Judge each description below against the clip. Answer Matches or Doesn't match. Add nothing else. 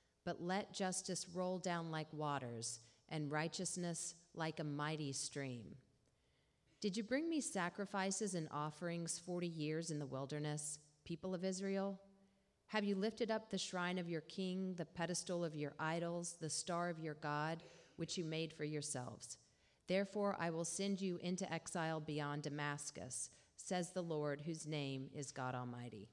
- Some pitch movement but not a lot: Matches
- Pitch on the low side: Doesn't match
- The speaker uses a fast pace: Doesn't match